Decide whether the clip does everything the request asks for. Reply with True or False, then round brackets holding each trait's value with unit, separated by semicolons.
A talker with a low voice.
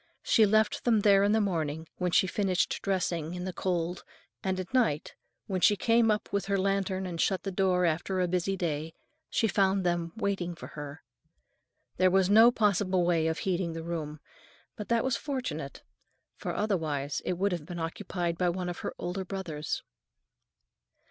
False (185 Hz)